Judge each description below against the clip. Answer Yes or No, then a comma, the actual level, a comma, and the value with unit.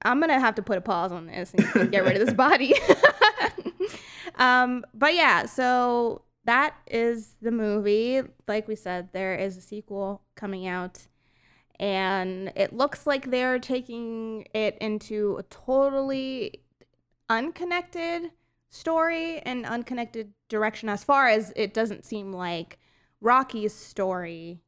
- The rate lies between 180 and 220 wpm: No, average, 140 wpm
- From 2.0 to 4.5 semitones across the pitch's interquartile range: No, average, 5.0 semitones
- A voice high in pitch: Yes, high, 225 Hz